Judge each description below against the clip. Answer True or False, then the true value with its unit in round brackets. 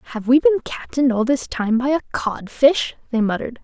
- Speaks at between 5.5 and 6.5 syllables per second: True (5.6 syllables/s)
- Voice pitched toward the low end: False (255 Hz)